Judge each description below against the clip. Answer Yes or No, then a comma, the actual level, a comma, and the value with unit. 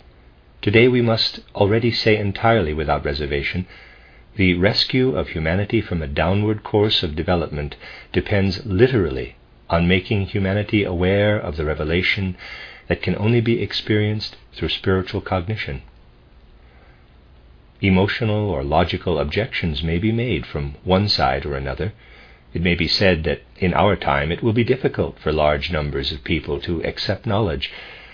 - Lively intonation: Yes, wide, 6.2 semitones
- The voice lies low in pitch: Yes, very low, 90 Hz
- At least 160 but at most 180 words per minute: No, average, 145 wpm